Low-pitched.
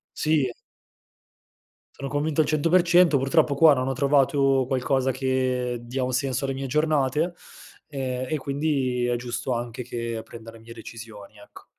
Yes: low, 130 Hz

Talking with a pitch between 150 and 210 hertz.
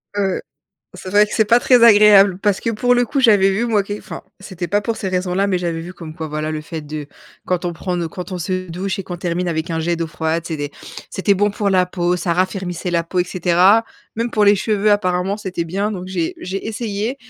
Yes: medium, 185 Hz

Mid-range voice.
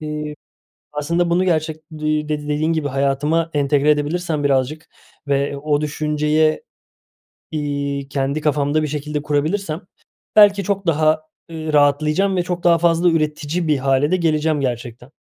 Yes: medium, 150 Hz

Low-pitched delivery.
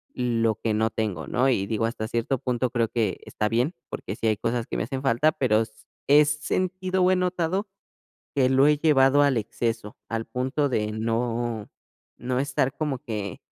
Yes: low, 125 Hz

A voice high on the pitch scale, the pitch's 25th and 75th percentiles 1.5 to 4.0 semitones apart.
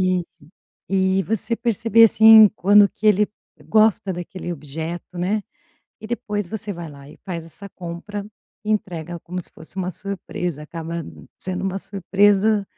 Yes: high, 195 Hz; average, 3.4 semitones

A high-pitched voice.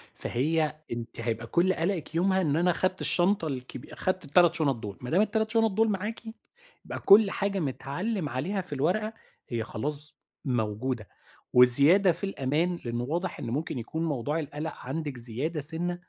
No: medium, 160 Hz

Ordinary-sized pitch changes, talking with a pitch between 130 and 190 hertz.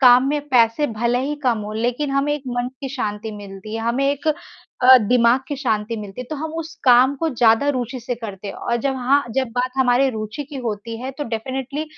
No: average, 3.5 semitones; very high, 250 Hz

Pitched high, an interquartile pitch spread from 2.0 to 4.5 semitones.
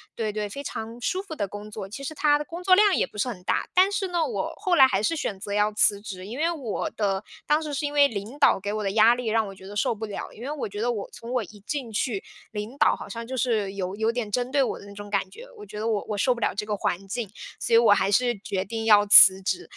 No: high, 220 Hz; average, 4.9 semitones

